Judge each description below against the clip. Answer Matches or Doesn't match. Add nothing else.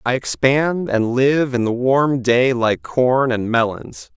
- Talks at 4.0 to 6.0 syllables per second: Doesn't match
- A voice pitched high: Doesn't match